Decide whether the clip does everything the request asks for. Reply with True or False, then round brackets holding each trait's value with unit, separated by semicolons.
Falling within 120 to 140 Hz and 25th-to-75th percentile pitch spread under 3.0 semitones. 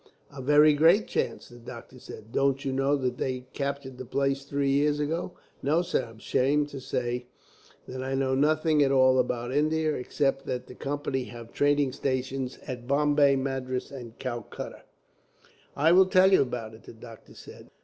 True (135 Hz; 2.4 semitones)